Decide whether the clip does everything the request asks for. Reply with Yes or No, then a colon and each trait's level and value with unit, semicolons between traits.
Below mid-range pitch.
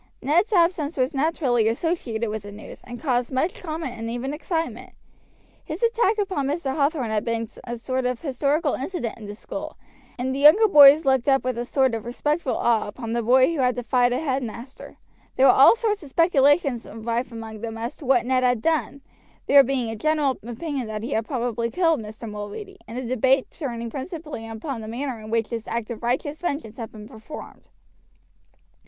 No: very high, 255 Hz